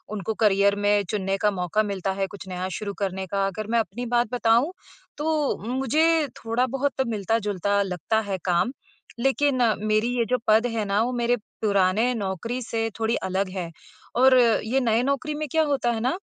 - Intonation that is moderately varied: Yes, average, 4.1 semitones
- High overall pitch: Yes, high, 220 Hz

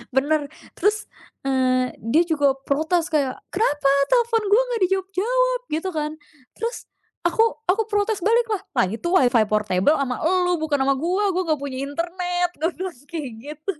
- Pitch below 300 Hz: No, very high, 335 Hz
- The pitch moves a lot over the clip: Yes, wide, 5.8 semitones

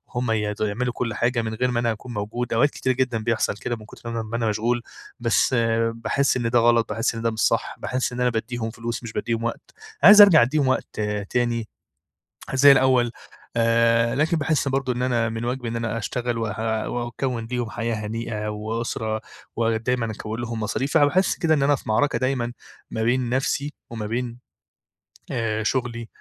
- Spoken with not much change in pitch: Yes, narrow, 1.9 semitones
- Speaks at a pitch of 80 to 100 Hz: No, low, 120 Hz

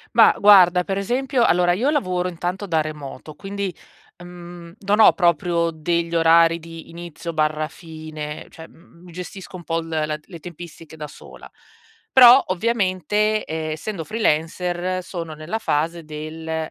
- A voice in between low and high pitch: Yes, medium, 170 Hz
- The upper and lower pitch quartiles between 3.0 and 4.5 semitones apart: No, narrow, 2.6 semitones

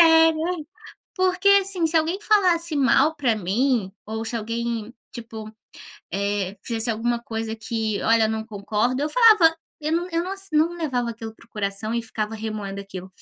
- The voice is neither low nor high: No, high, 235 Hz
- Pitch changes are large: Yes, wide, 6.9 semitones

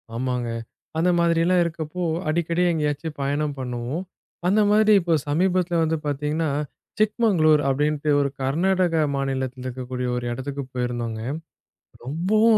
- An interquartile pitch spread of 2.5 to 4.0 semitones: No, average, 4.7 semitones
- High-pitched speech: No, medium, 150 Hz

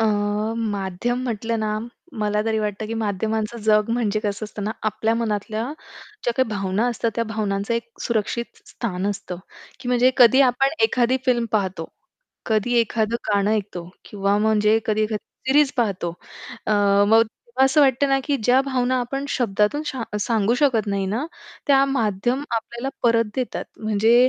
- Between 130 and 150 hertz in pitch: No, high, 220 Hz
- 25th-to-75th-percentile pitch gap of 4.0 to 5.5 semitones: No, average, 2.7 semitones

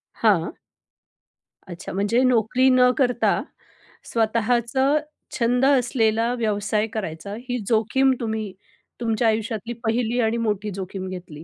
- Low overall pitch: No, high, 225 Hz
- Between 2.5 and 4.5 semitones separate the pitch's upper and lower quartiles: Yes, average, 2.9 semitones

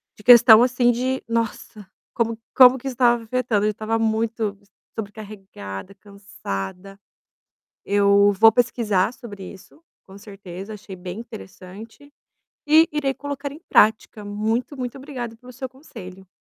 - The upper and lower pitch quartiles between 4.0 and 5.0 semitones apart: No, average, 3.6 semitones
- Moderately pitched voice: No, high, 220 Hz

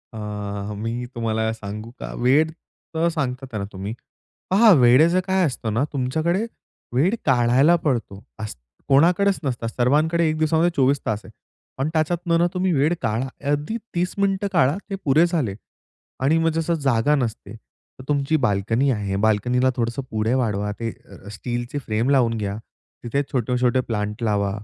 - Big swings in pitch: Yes, wide, 5.9 semitones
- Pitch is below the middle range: Yes, low, 130 Hz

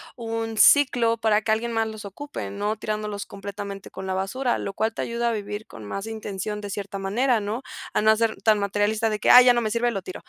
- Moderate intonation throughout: No, narrow, 2.1 semitones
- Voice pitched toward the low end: No, high, 215 Hz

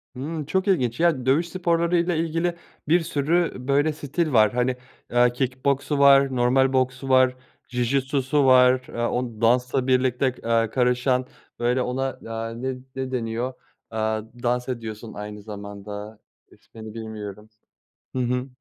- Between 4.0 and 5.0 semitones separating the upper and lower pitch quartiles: No, average, 3.0 semitones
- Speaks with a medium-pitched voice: No, low, 130 Hz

